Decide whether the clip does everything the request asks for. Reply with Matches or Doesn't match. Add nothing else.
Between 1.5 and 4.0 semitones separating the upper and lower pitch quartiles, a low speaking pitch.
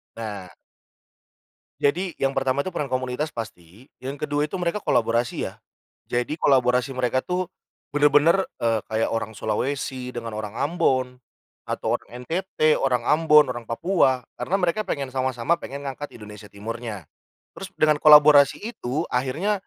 Doesn't match